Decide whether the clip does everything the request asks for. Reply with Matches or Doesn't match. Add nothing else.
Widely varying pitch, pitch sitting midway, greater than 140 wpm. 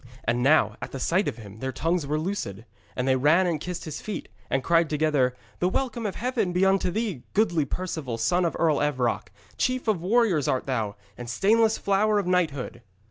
Matches